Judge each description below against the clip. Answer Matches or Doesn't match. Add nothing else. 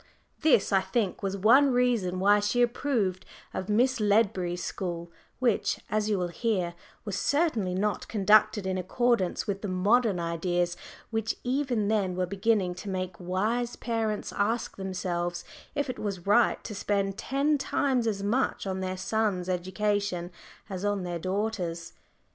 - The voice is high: Matches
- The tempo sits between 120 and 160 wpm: Matches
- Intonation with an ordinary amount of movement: Matches